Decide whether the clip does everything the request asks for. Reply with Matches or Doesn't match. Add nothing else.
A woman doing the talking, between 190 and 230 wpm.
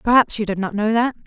Doesn't match